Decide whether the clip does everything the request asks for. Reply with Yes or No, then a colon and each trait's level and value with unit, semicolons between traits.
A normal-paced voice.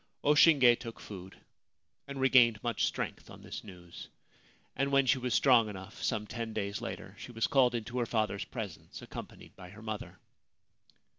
Yes: average, 170 wpm